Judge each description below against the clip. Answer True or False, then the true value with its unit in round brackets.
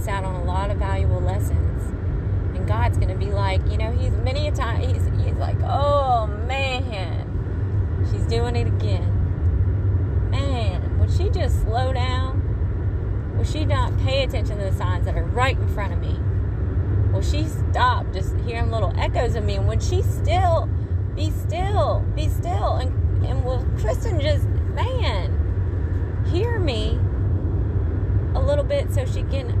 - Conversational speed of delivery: True (160 wpm)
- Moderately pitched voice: False (95 Hz)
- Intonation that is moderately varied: False (1.2 semitones)